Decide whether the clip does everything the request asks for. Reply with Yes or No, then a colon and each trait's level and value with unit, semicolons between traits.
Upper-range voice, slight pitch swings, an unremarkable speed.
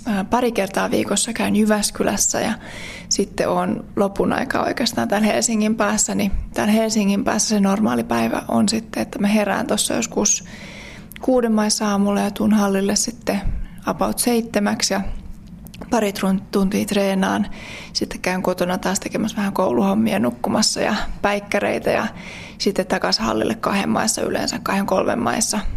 Yes: high, 205 Hz; narrow, 1.9 semitones; average, 140 wpm